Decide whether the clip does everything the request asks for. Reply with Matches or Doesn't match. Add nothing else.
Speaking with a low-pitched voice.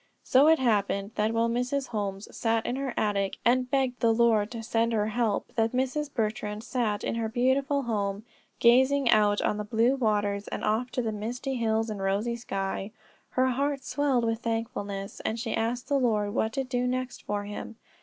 Doesn't match